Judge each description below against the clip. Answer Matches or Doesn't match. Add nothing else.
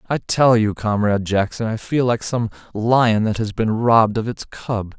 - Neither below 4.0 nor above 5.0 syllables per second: Matches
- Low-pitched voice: Matches